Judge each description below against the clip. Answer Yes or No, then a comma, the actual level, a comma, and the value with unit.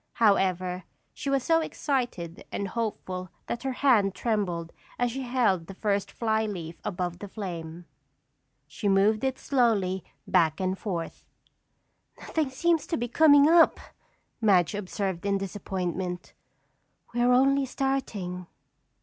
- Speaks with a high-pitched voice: Yes, high, 205 Hz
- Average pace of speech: No, slow, 130 wpm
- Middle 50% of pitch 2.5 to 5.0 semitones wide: No, wide, 5.4 semitones